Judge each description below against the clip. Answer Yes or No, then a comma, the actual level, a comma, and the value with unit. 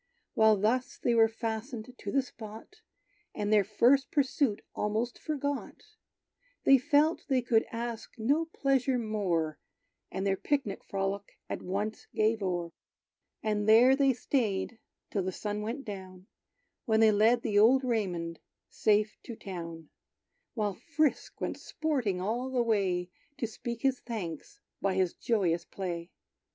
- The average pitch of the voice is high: Yes, high, 220 Hz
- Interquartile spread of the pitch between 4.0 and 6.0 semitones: Yes, average, 4.3 semitones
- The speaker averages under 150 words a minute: Yes, average, 140 wpm